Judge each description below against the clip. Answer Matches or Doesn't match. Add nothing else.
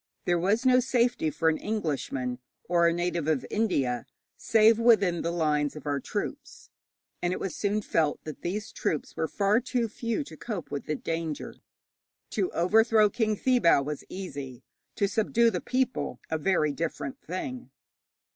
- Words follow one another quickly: Doesn't match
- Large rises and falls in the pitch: Matches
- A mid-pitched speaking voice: Matches